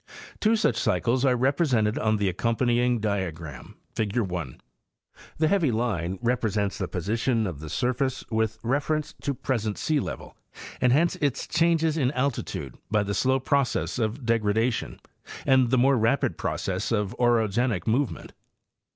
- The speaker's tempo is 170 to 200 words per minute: No, average, 145 wpm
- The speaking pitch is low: Yes, low, 120 Hz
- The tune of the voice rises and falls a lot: No, average, 4.2 semitones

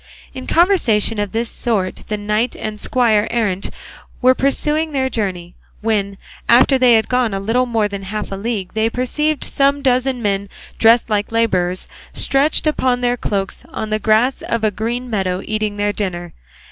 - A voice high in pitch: Yes, high, 225 Hz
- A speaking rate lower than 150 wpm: No, average, 170 wpm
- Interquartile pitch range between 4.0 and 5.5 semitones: No, average, 3.5 semitones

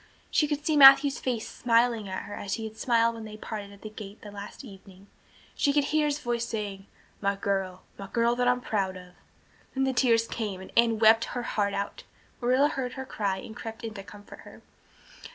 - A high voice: Yes, high, 225 Hz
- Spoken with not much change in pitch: No, average, 3.7 semitones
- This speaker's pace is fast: Yes, fast, 210 wpm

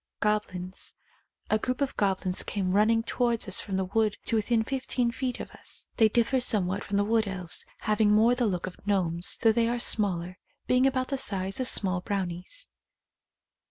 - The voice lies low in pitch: No, high, 210 Hz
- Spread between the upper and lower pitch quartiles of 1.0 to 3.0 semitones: No, average, 3.8 semitones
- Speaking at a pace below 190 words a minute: No, average, 195 wpm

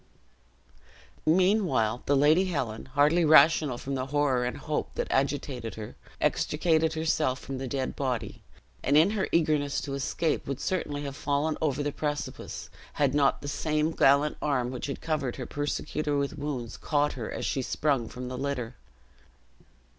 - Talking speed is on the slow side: No, average, 160 wpm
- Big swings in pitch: No, narrow, 2.6 semitones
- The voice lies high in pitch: No, medium, 145 Hz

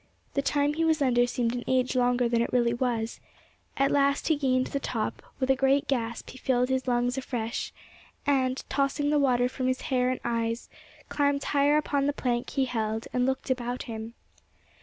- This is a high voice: Yes, very high, 255 Hz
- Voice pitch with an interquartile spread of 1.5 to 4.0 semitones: Yes, narrow, 2.4 semitones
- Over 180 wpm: Yes, average, 195 wpm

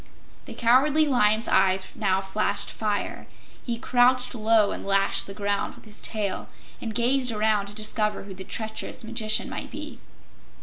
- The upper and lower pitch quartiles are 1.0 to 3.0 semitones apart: Yes, average, 2.7 semitones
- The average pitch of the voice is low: No, high, 215 Hz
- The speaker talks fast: No, average, 160 wpm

